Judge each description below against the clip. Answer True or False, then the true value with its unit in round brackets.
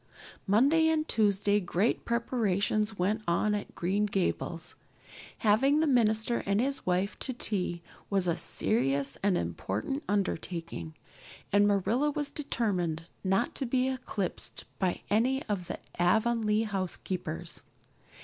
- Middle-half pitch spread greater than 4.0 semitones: True (4.5 semitones)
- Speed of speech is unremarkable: False (125 wpm)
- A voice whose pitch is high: True (205 Hz)